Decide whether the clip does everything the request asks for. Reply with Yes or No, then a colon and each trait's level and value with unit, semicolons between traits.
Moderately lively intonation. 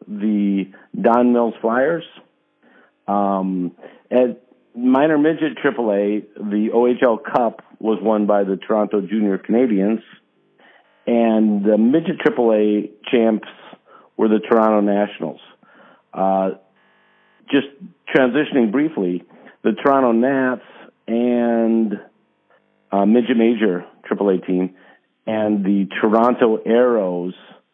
Yes: average, 3.0 semitones